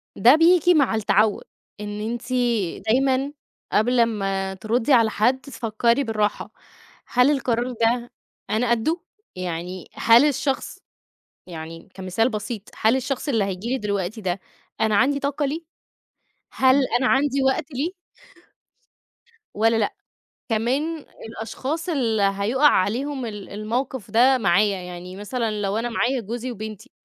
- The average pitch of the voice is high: Yes, high, 230 Hz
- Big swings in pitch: No, average, 4.2 semitones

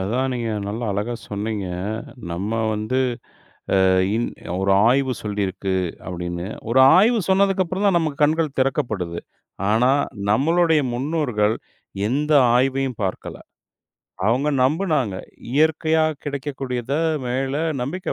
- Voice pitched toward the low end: Yes, low, 130 Hz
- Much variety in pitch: Yes, wide, 6.3 semitones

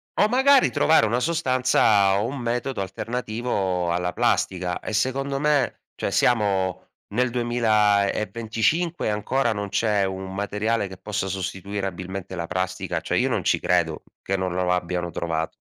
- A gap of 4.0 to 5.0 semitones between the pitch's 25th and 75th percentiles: Yes, average, 4.6 semitones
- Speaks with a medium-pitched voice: No, low, 105 Hz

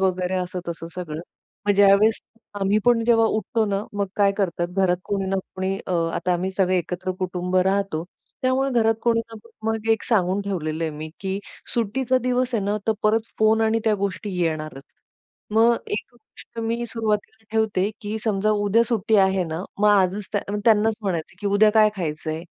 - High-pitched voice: Yes, high, 205 Hz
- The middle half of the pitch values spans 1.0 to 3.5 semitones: Yes, average, 3.2 semitones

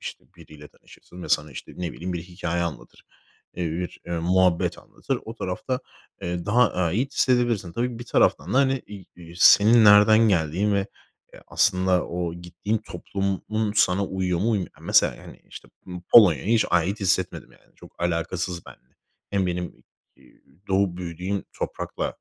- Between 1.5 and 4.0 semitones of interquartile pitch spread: Yes, average, 3.2 semitones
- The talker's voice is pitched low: Yes, very low, 95 Hz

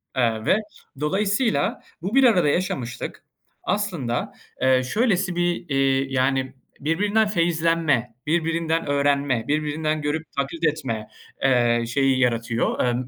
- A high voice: No, medium, 145 Hz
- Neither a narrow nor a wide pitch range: Yes, average, 4.9 semitones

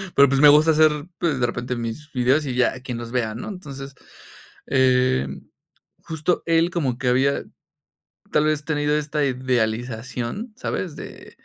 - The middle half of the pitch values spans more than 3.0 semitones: Yes, average, 3.5 semitones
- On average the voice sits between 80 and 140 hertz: Yes, low, 135 Hz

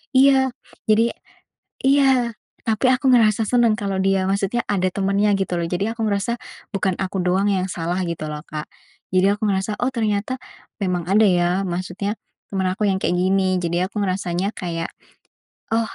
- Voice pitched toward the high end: Yes, high, 195 Hz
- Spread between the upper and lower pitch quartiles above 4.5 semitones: No, average, 3.2 semitones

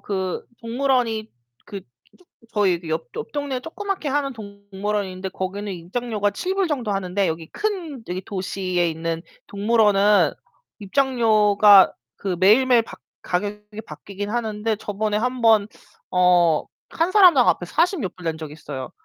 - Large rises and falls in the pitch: No, average, 4.8 semitones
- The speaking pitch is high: Yes, high, 210 Hz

